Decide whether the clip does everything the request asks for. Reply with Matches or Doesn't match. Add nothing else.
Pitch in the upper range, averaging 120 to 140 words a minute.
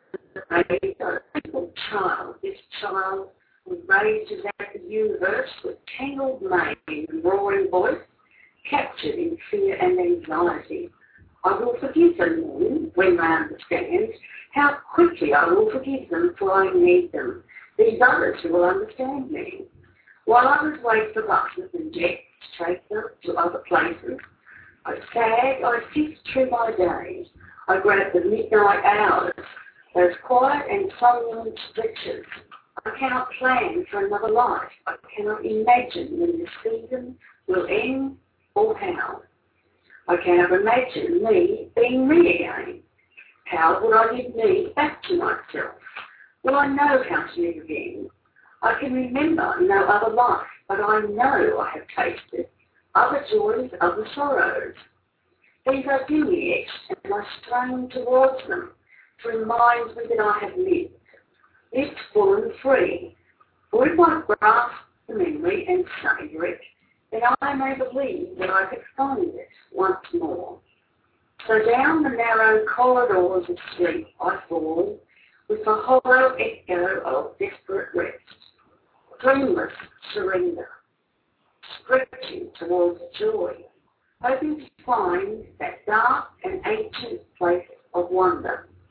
Matches